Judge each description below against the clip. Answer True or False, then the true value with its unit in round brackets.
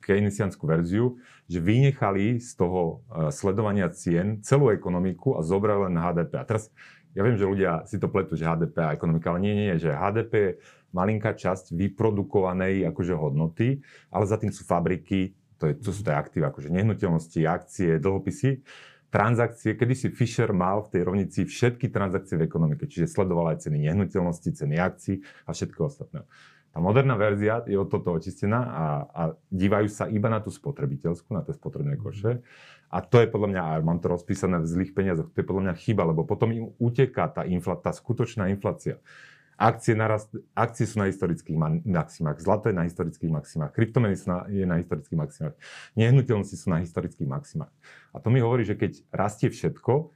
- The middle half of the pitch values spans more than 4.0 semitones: True (4.4 semitones)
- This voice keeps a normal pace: False (185 wpm)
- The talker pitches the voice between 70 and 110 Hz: True (100 Hz)